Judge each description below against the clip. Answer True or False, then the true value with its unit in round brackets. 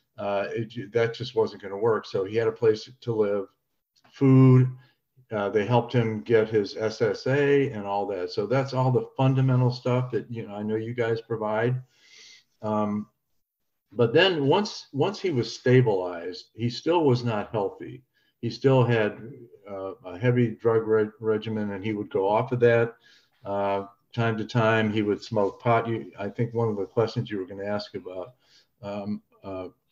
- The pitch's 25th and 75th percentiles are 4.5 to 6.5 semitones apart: False (3.1 semitones)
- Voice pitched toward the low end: True (115 Hz)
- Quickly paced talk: False (185 wpm)